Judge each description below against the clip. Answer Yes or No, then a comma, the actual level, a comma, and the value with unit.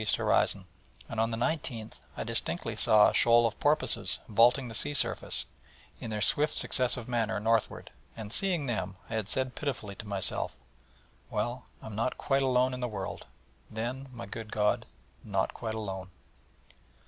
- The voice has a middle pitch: No, low, 115 Hz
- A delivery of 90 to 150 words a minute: No, average, 165 wpm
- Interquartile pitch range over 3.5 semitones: No, average, 3.2 semitones